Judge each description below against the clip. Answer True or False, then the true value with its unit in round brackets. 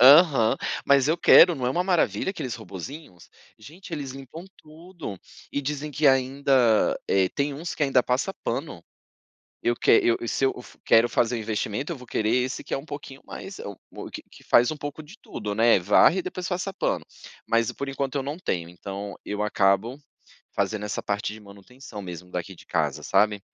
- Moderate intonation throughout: False (5.8 semitones)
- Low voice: True (130 Hz)